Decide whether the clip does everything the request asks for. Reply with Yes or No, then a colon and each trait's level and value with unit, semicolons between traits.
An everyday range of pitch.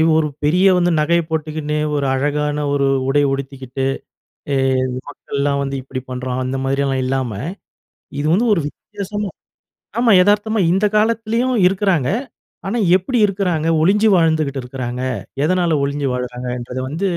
No: wide, 5.8 semitones